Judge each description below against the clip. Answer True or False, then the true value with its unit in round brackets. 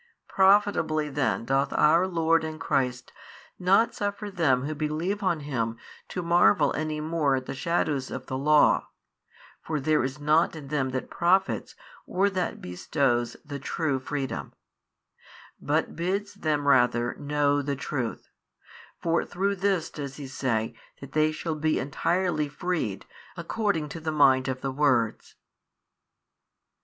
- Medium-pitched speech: True (150 Hz)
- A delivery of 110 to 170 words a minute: True (145 wpm)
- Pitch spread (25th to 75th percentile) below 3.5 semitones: False (4.1 semitones)